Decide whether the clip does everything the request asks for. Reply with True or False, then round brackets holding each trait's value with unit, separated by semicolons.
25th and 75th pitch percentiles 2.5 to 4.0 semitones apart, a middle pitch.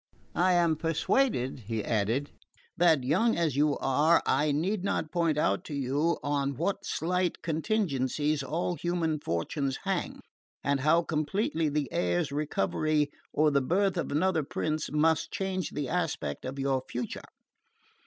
True (3.6 semitones; 150 Hz)